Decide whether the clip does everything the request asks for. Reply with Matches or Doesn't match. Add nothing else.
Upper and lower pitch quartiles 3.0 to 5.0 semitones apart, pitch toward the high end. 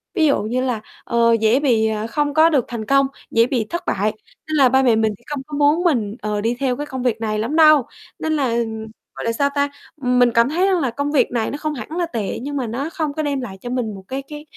Matches